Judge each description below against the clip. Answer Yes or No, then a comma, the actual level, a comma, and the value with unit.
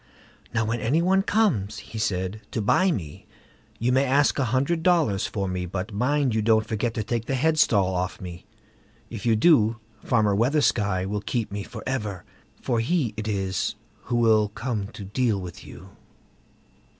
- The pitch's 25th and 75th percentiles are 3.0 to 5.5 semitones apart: Yes, average, 4.4 semitones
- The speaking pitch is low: Yes, low, 110 Hz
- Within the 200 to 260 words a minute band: No, average, 175 wpm